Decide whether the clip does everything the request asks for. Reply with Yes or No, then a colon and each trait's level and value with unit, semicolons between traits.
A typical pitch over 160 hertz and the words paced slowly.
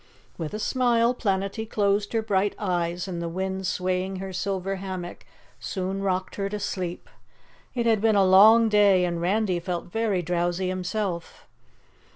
No: high, 190 Hz; average, 160 wpm